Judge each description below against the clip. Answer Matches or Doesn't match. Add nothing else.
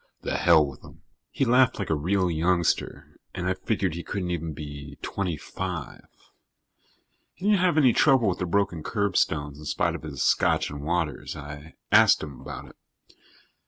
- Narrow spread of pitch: Doesn't match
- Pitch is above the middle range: Doesn't match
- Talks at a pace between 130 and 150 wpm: Doesn't match